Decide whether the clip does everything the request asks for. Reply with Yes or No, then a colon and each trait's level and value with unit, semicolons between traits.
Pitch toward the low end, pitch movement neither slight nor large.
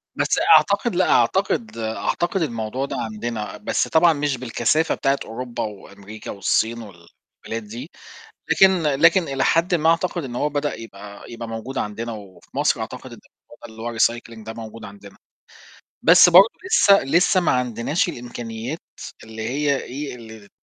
No: low, 120 Hz; wide, 6.3 semitones